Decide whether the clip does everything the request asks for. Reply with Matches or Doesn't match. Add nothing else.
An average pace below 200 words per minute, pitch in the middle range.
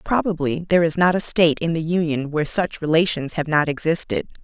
Doesn't match